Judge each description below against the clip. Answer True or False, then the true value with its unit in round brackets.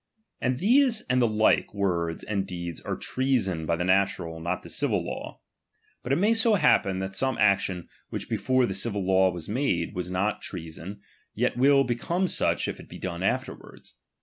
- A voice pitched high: False (100 Hz)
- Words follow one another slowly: False (185 wpm)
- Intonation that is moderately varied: False (6.2 semitones)